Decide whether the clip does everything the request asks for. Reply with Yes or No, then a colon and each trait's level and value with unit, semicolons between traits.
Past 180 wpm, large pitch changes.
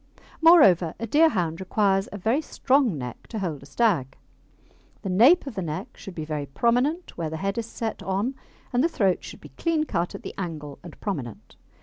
Yes: average, 200 wpm; wide, 6.9 semitones